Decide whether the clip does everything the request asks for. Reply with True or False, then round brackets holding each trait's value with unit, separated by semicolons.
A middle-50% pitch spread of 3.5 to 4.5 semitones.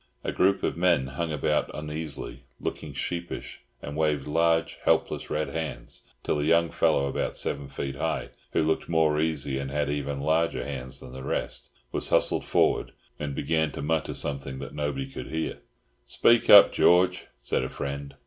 False (2.8 semitones)